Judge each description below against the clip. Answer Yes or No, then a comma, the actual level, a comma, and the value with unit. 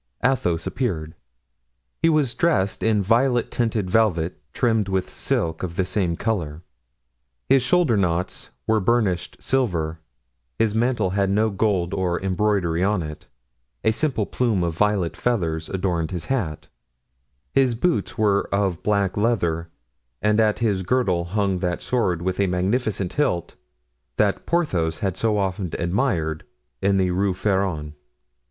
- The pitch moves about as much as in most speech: Yes, average, 4.3 semitones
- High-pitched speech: No, low, 100 Hz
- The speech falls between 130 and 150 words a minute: Yes, average, 145 wpm